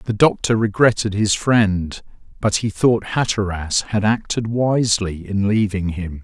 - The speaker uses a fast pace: No, average, 145 wpm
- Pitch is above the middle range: No, low, 105 Hz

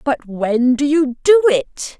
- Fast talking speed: No, average, 180 wpm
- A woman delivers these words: Yes, female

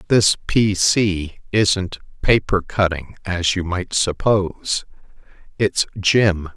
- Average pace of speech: No, slow, 110 wpm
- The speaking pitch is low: Yes, very low, 95 Hz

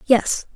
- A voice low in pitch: No, high, 240 Hz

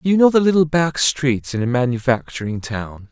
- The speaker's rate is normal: No, fast, 210 wpm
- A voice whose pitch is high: No, low, 135 Hz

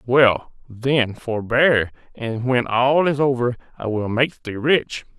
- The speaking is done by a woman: No, male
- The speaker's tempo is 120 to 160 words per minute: Yes, average, 150 wpm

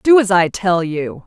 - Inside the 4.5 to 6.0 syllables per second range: No, 4.1 syllables/s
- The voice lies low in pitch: No, high, 190 Hz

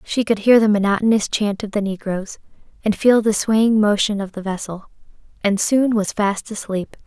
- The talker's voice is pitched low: No, high, 210 Hz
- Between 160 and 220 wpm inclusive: Yes, average, 185 wpm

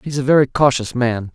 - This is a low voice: Yes, low, 130 Hz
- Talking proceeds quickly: Yes, fast, 225 wpm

